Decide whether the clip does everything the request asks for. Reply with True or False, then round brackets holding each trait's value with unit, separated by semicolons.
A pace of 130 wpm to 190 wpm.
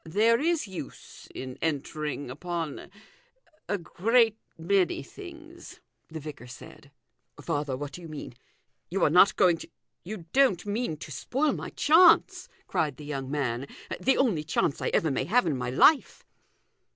True (170 wpm)